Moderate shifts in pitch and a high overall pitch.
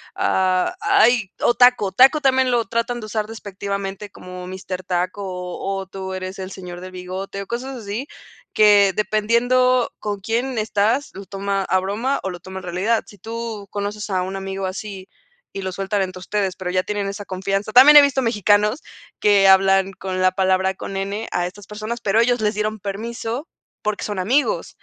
Yes: average, 3.2 semitones; high, 200 Hz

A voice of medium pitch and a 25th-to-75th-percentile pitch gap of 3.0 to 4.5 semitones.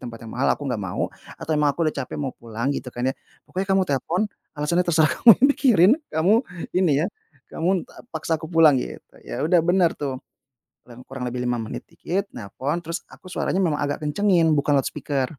No: medium, 150 Hz; average, 5.0 semitones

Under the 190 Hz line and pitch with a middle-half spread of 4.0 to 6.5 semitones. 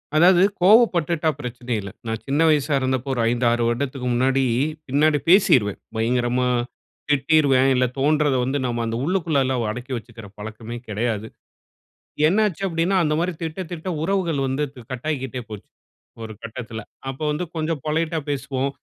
Yes: low, 135 Hz; average, 4.6 semitones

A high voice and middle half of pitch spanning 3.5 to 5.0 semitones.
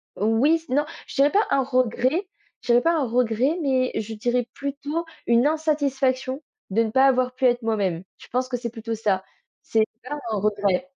Yes: very high, 255 Hz; average, 3.8 semitones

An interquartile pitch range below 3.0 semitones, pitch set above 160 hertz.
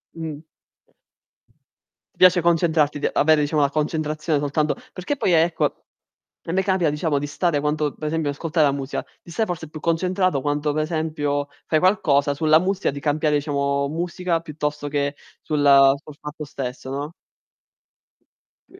No: narrow, 2.4 semitones; medium, 155 Hz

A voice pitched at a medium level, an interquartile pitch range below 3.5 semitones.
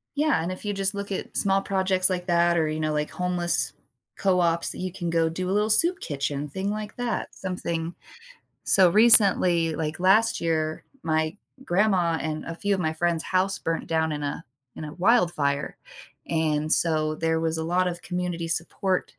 Yes: medium, 175 Hz; average, 3.0 semitones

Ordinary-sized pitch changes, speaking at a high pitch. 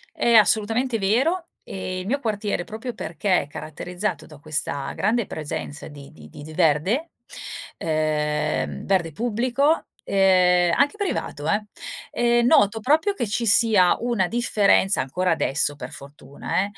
No: wide, 7.2 semitones; high, 195 Hz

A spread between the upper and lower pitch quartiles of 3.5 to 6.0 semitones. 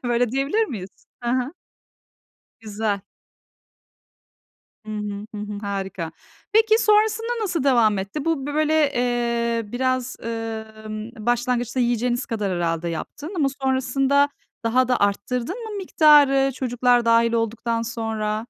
Yes: average, 3.9 semitones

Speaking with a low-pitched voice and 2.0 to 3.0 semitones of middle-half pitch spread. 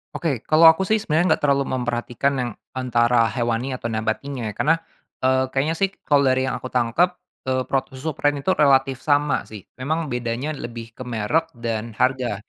No: low, 130 Hz; average, 3.6 semitones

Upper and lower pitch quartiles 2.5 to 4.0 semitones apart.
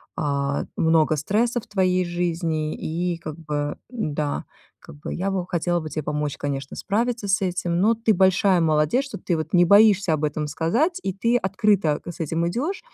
No: average, 4.5 semitones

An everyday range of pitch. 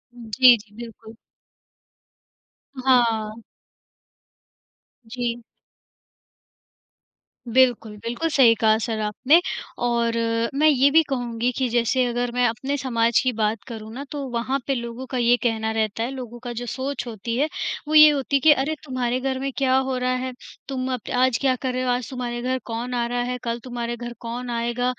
No: narrow, 2.0 semitones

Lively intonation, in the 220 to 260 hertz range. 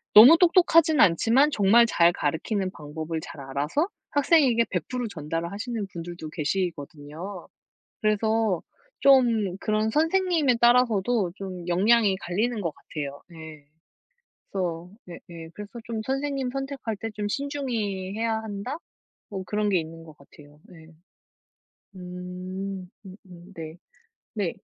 No: wide, 5.7 semitones; high, 200 Hz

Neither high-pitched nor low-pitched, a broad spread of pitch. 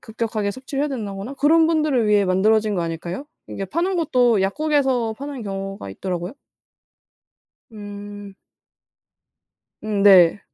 No: high, 215 Hz; wide, 5.7 semitones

